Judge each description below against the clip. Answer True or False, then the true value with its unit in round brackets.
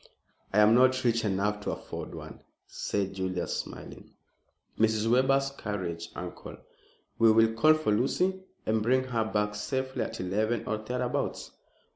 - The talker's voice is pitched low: True (110 Hz)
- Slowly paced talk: False (145 wpm)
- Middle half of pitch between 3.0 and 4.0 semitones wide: True (3.7 semitones)